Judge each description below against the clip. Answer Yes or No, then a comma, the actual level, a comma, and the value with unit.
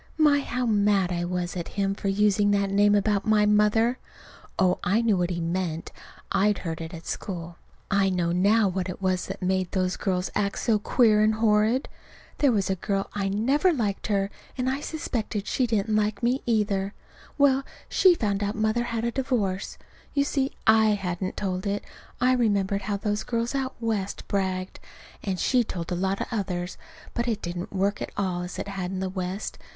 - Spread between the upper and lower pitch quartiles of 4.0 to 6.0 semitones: No, average, 3.1 semitones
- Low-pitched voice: No, high, 200 Hz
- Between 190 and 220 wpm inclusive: Yes, average, 200 wpm